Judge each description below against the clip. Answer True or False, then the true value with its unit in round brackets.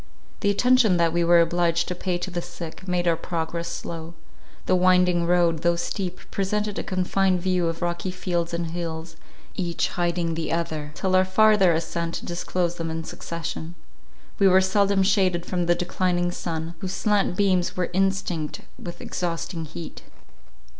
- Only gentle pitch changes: True (1.7 semitones)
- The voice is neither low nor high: True (175 Hz)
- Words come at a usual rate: True (165 wpm)